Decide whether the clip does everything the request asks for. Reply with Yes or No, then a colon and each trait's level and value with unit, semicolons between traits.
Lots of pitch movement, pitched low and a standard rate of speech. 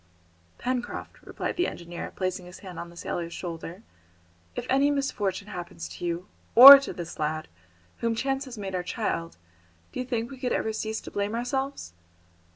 No: wide, 6.5 semitones; high, 205 Hz; average, 175 wpm